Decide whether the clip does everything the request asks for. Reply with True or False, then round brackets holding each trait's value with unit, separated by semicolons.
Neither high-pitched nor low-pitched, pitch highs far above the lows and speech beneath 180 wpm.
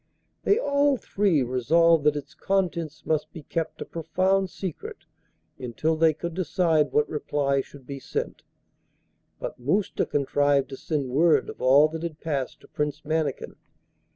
False (155 Hz; 3.2 semitones; 155 wpm)